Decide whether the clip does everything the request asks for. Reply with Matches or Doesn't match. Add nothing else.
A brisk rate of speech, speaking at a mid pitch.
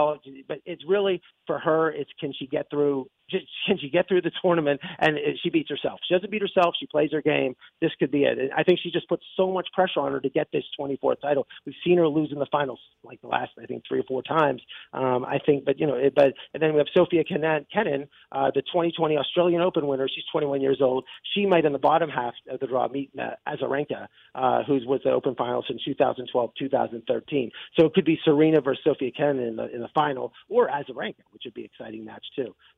Matches